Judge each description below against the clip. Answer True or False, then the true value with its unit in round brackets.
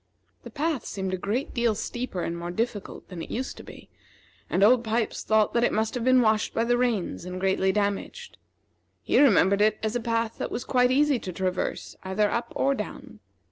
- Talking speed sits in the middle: False (210 wpm)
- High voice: True (220 Hz)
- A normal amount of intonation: True (4.1 semitones)